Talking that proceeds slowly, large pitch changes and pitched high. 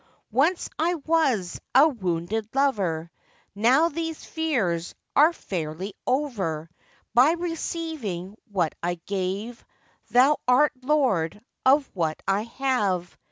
Yes: slow, 110 wpm; wide, 8.5 semitones; high, 230 Hz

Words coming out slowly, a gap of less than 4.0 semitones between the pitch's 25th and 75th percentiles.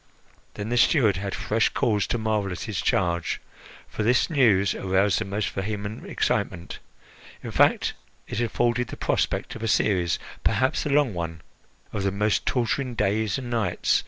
No: average, 165 wpm; average, 3.5 semitones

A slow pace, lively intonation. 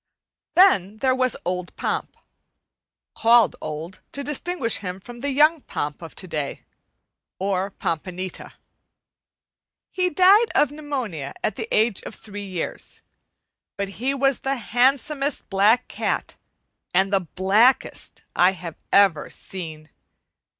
Yes: slow, 125 wpm; wide, 6.8 semitones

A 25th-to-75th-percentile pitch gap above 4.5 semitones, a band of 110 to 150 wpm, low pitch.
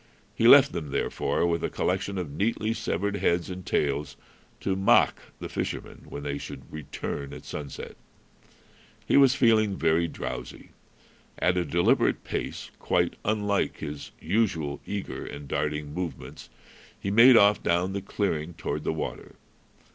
Yes: average, 5.2 semitones; average, 145 wpm; very low, 90 Hz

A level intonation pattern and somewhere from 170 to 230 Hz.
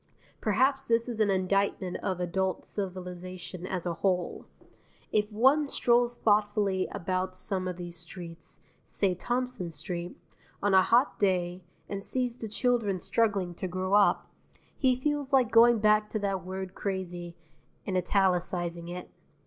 No: average, 3.5 semitones; high, 190 Hz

